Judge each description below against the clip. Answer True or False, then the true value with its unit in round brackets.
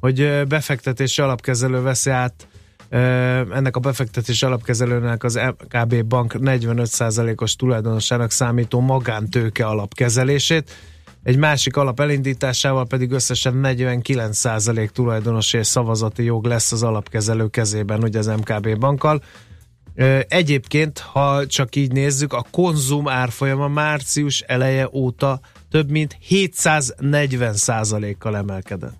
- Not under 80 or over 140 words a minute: True (105 wpm)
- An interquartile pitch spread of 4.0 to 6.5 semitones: False (3.1 semitones)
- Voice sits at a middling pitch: False (125 Hz)